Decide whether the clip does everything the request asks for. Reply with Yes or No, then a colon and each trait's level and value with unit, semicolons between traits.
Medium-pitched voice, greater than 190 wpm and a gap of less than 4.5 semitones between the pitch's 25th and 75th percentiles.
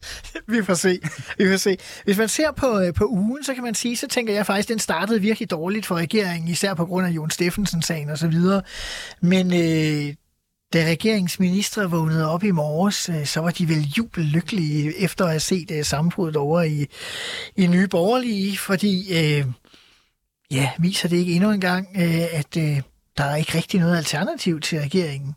No: medium, 180 Hz; average, 175 wpm; average, 3.8 semitones